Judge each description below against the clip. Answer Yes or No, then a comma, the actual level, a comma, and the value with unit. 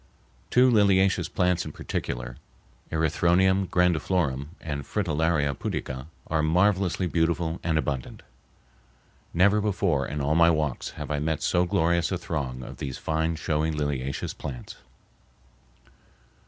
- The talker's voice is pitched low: Yes, very low, 80 Hz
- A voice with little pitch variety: No, average, 3.7 semitones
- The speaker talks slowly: Yes, slow, 125 wpm